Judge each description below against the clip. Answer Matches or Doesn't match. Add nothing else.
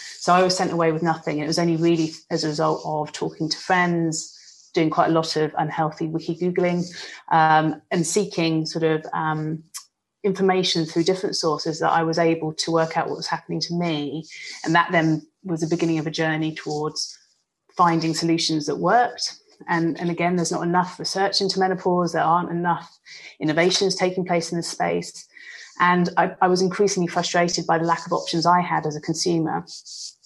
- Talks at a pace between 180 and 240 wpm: Matches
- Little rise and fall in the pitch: Matches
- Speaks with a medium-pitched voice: Matches